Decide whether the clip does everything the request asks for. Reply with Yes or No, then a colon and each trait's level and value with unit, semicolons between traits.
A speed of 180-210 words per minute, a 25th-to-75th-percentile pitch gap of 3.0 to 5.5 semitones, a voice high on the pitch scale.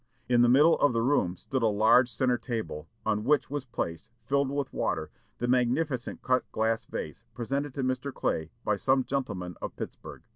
No: average, 185 wpm; average, 3.5 semitones; low, 125 Hz